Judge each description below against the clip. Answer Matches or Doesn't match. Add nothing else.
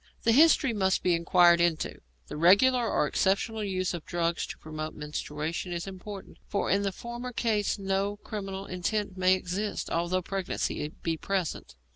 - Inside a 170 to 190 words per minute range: Doesn't match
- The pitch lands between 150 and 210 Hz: Matches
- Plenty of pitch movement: Doesn't match